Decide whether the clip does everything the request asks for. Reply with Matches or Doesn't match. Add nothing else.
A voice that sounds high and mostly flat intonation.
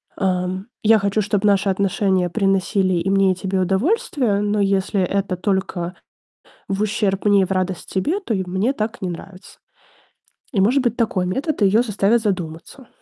Matches